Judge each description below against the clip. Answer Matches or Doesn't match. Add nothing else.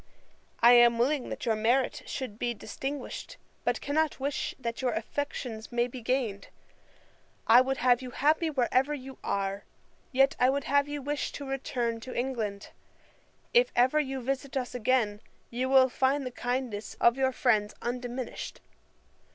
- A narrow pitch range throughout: Matches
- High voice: Matches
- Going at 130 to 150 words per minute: Doesn't match